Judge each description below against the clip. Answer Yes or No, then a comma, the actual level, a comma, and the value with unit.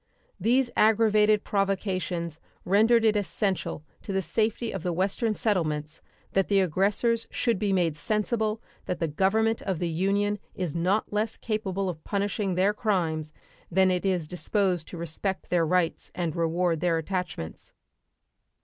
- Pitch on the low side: No, high, 190 Hz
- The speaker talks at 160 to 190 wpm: No, average, 150 wpm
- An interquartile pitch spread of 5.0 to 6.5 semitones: No, average, 3.5 semitones